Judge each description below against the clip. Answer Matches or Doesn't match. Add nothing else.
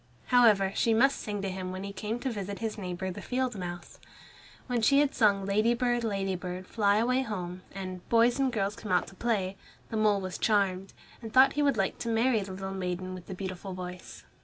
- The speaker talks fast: Matches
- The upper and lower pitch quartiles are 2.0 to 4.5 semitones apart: Matches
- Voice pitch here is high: Matches